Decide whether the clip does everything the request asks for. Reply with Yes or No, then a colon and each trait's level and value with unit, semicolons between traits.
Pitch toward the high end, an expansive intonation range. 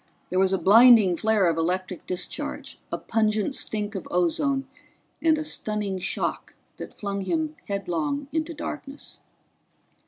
Yes: high, 210 Hz; wide, 6.7 semitones